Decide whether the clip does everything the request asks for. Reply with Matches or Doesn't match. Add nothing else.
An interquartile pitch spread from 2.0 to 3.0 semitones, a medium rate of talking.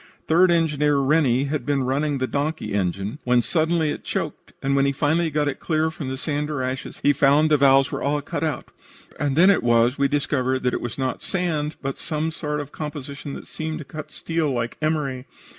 Doesn't match